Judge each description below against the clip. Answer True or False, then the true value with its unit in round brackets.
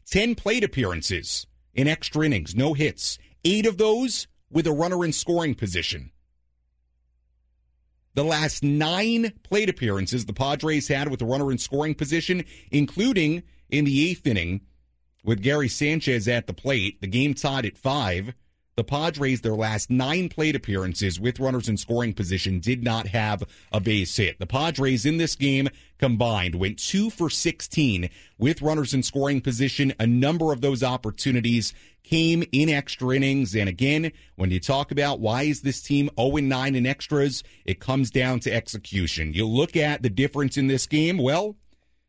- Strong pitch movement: True (6.1 semitones)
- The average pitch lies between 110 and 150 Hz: True (135 Hz)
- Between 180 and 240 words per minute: False (165 wpm)